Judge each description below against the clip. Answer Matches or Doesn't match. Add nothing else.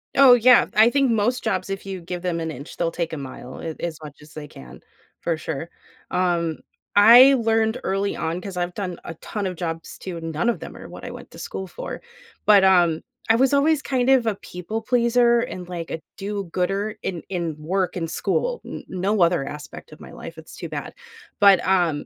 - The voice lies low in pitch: Doesn't match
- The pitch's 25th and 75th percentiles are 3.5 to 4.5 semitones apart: Doesn't match